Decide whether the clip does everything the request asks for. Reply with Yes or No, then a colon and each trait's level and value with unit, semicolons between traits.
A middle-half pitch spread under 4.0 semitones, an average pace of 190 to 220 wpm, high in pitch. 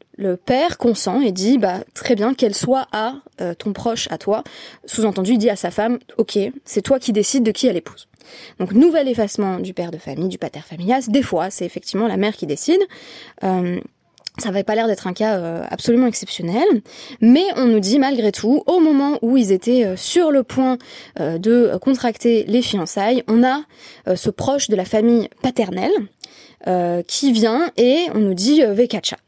No: average, 4.8 semitones; average, 200 wpm; high, 225 Hz